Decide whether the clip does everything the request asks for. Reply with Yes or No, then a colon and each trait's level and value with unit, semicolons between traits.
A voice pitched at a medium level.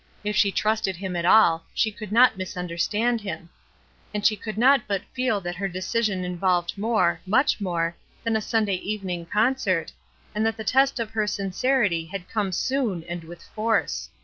No: high, 205 Hz